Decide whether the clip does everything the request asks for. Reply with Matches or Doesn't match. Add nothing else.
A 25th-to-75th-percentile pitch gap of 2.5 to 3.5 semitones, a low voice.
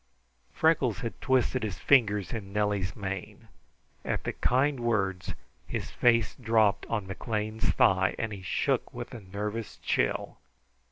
Matches